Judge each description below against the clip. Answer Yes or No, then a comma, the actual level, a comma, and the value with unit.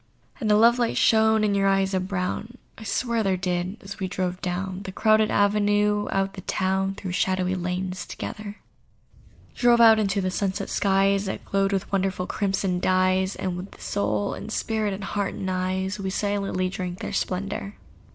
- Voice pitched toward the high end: Yes, high, 195 Hz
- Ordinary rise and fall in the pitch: No, narrow, 1.8 semitones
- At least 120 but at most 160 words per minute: No, average, 180 wpm